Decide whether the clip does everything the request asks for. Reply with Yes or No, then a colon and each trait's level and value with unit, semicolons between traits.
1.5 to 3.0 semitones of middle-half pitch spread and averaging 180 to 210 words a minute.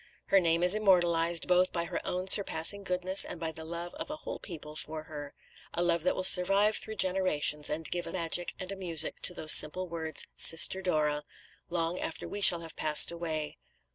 Yes: narrow, 2.5 semitones; average, 200 wpm